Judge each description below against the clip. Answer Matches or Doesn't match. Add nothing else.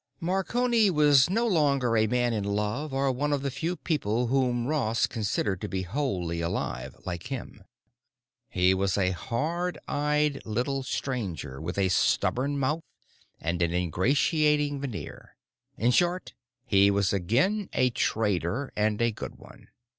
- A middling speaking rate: Matches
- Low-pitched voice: Matches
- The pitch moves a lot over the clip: Matches